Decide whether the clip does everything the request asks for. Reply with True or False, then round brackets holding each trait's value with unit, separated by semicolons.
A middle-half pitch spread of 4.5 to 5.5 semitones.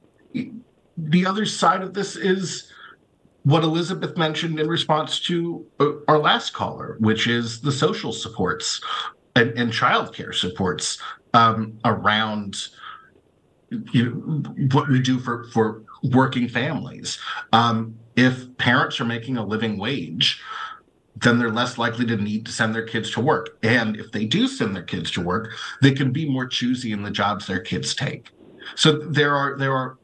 True (5.2 semitones)